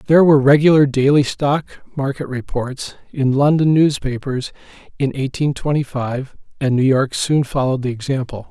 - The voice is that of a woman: No, male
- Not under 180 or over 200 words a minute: No, average, 150 wpm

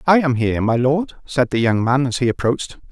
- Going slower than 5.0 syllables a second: No, 5.8 syllables/s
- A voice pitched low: Yes, low, 130 Hz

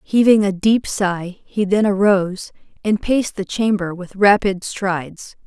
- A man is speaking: No, female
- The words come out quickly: No, average, 155 wpm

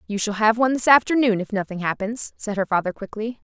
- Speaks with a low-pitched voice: No, high, 215 Hz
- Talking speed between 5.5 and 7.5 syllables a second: Yes, 6.2 syllables/s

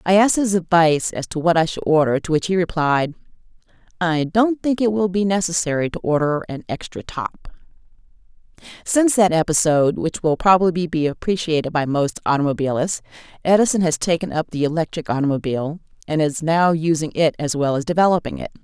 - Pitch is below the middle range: No, medium, 165 Hz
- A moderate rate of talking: Yes, average, 175 wpm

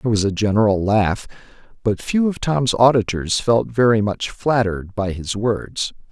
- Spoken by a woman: No, male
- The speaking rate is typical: Yes, average, 165 wpm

